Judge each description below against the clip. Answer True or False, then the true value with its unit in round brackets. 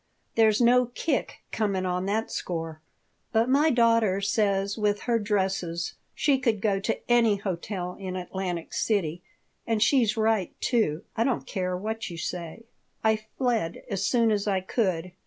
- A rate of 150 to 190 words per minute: True (155 wpm)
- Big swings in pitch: False (3.7 semitones)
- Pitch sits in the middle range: False (205 Hz)